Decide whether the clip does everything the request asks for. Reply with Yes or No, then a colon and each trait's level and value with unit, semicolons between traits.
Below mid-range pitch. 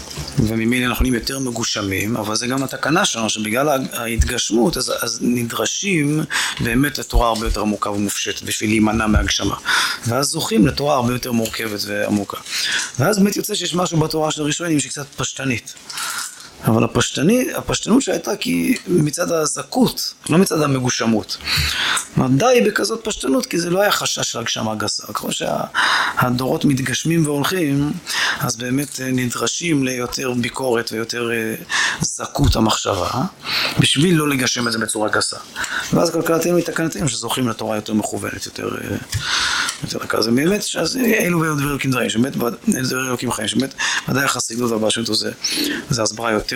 Yes: low, 130 Hz